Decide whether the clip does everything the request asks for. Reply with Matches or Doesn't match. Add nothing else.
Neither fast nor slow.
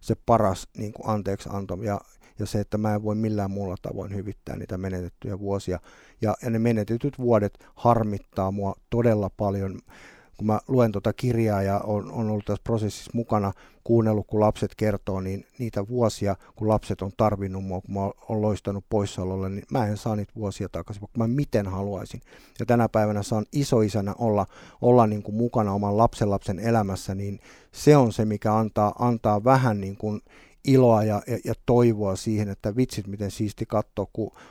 Doesn't match